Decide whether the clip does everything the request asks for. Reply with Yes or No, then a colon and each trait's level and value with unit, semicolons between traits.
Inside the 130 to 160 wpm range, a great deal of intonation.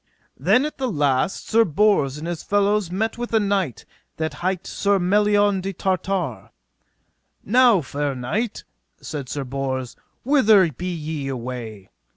Yes: average, 145 wpm; wide, 6.9 semitones